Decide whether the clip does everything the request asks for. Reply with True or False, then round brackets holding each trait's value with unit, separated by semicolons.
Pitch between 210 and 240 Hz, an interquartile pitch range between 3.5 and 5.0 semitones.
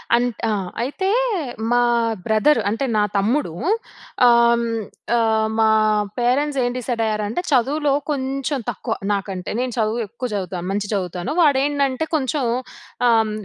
True (235 Hz; 4.2 semitones)